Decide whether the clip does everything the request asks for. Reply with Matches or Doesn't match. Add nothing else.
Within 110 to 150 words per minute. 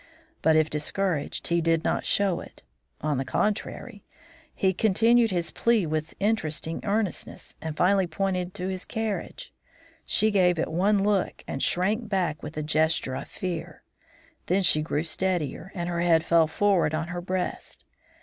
Doesn't match